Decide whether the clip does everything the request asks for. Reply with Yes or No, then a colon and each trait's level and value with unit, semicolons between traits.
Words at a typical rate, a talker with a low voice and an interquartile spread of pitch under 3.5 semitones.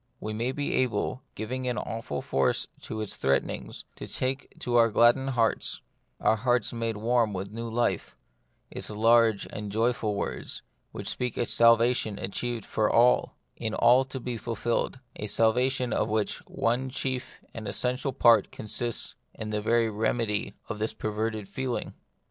Yes: average, 175 wpm; low, 115 Hz; narrow, 2.4 semitones